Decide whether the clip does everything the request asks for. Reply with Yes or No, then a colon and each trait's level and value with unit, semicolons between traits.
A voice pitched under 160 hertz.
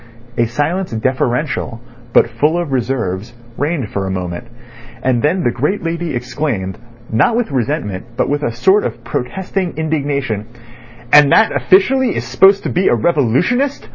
Yes: medium, 140 Hz